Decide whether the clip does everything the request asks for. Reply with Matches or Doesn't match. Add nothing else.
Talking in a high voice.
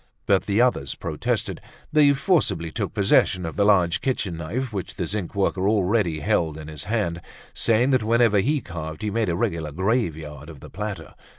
Doesn't match